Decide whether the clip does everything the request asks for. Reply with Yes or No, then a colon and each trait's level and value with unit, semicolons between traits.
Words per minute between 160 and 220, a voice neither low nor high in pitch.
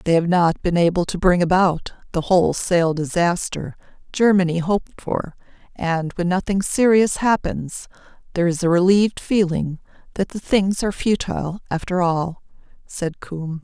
No: average, 145 wpm; medium, 180 Hz